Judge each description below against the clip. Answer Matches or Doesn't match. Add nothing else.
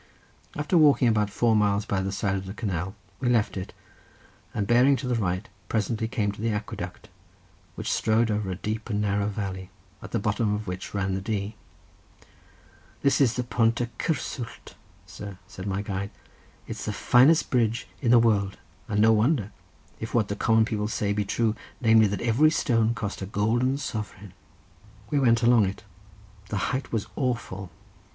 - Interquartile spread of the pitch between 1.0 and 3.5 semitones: Matches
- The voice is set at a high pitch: Doesn't match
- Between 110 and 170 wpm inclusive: Doesn't match